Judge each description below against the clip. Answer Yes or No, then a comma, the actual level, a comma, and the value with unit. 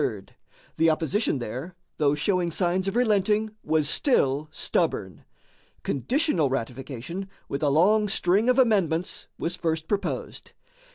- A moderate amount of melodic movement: No, wide, 5.7 semitones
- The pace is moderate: No, slow, 120 wpm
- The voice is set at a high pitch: No, medium, 170 Hz